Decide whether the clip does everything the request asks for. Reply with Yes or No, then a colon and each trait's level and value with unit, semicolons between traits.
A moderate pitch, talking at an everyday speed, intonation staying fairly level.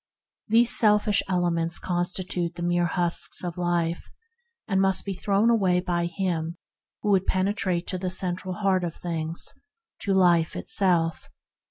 Yes: medium, 180 Hz; average, 150 wpm; narrow, 2.0 semitones